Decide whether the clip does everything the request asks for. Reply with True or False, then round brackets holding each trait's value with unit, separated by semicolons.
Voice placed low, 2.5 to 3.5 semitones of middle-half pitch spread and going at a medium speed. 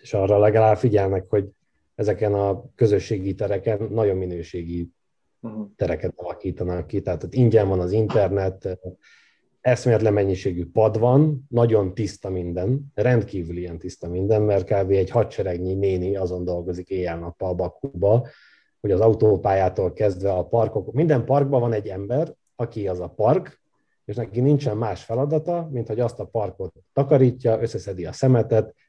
False (105 Hz; 4.0 semitones; 145 wpm)